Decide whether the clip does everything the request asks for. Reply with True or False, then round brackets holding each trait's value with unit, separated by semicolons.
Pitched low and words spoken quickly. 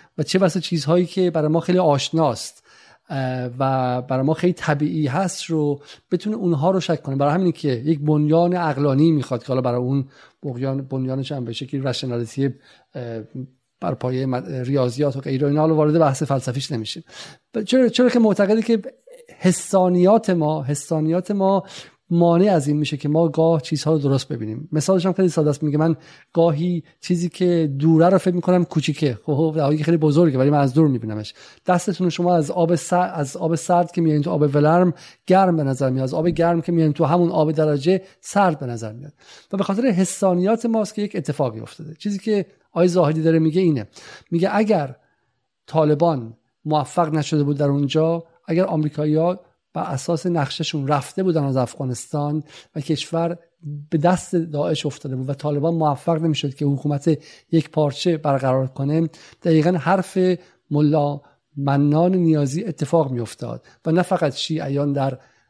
False (155 Hz; 170 wpm)